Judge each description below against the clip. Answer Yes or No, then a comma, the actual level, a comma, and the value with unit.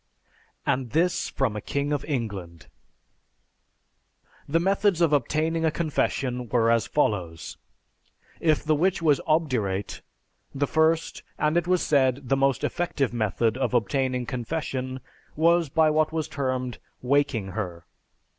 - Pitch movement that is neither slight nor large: Yes, average, 4.8 semitones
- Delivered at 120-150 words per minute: Yes, slow, 135 wpm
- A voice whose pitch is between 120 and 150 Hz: Yes, medium, 140 Hz